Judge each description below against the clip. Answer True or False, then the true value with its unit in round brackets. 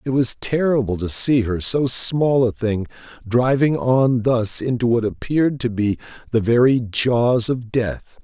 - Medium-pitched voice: False (120 Hz)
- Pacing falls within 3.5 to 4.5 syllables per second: True (4.1 syllables/s)